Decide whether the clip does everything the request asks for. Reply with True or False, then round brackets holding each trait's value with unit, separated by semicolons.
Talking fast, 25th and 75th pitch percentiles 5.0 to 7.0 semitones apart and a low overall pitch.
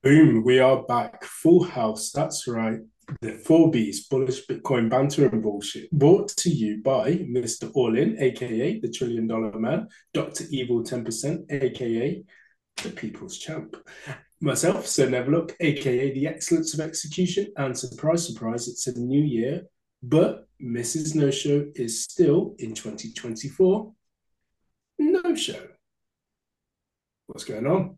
False (135 wpm; 5.6 semitones; 130 Hz)